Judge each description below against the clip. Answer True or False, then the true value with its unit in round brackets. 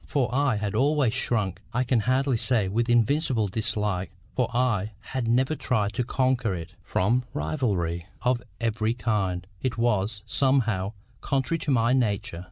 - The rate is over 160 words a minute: False (155 wpm)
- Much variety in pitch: False (3.9 semitones)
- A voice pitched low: True (115 Hz)